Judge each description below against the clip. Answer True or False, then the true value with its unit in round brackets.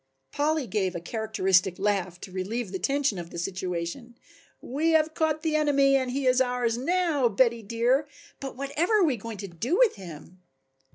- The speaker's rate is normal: True (180 wpm)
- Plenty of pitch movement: True (7.0 semitones)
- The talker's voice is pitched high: True (240 Hz)